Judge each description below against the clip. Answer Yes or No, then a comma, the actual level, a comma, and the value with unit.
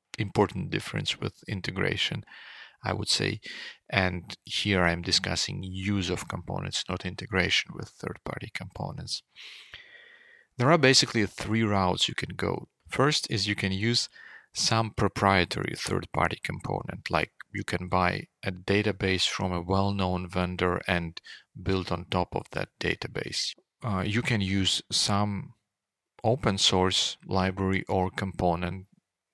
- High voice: No, very low, 95 Hz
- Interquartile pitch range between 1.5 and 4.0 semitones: Yes, narrow, 2.4 semitones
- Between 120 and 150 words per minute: Yes, slow, 135 wpm